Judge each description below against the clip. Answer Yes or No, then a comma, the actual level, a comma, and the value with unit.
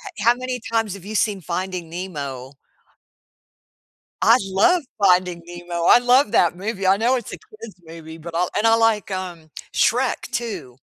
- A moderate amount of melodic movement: Yes, average, 4.8 semitones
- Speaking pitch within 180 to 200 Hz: Yes, high, 190 Hz